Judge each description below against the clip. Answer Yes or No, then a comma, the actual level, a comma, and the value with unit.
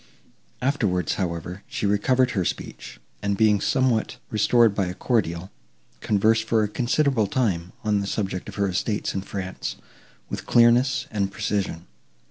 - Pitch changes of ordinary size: Yes, average, 3.6 semitones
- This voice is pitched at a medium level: No, low, 105 Hz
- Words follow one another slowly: No, average, 145 wpm